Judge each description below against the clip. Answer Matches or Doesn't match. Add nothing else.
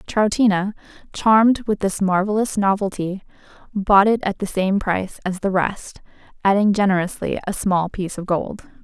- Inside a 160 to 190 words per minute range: Doesn't match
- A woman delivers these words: Matches